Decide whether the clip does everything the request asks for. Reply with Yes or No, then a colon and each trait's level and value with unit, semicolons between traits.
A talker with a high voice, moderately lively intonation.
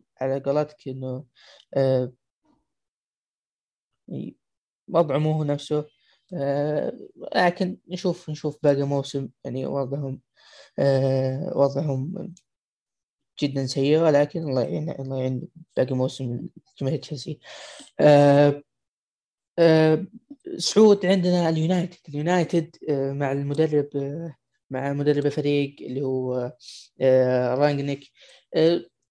No: medium, 145 Hz; average, 3.5 semitones